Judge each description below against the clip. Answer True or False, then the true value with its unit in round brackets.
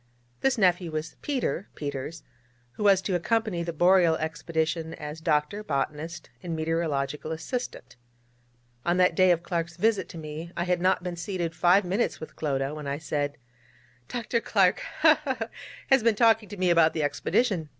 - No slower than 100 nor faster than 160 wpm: False (170 wpm)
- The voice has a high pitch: False (170 Hz)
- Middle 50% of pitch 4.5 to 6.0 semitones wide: False (3.8 semitones)